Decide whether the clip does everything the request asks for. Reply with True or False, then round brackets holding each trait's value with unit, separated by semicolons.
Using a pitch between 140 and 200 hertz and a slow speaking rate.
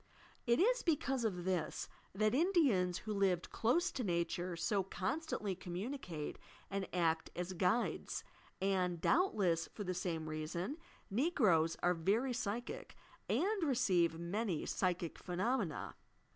True (190 Hz; 125 wpm)